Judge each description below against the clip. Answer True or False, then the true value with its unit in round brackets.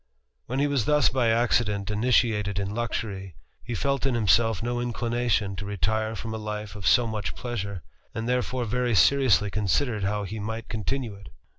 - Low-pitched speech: True (110 Hz)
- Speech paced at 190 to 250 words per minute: False (170 wpm)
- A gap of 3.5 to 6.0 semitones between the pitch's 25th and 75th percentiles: False (2.8 semitones)